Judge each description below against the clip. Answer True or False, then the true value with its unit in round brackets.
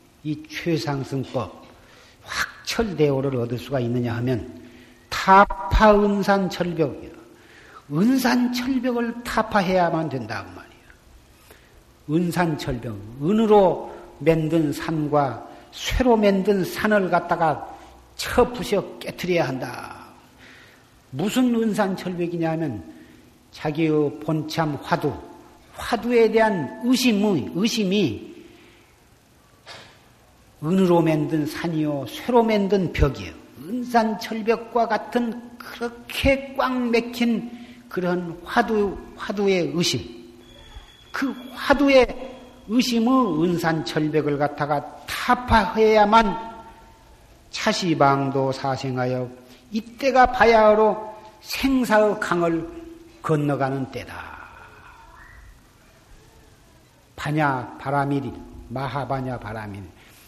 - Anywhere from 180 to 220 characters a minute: True (200 characters per minute)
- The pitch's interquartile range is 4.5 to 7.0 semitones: False (8.3 semitones)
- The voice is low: False (175 Hz)